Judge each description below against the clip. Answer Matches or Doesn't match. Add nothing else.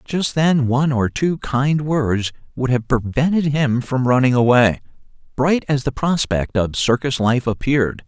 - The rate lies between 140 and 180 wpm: Matches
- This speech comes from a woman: Doesn't match